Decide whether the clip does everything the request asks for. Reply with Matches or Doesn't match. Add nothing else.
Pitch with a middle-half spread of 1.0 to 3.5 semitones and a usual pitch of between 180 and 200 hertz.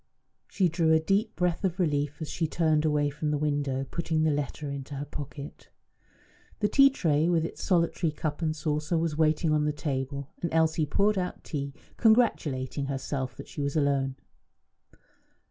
Doesn't match